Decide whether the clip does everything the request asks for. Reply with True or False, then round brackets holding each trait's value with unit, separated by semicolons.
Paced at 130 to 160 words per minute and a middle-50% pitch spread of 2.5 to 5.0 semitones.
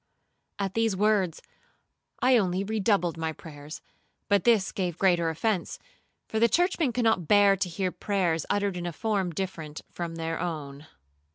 True (150 wpm; 4.0 semitones)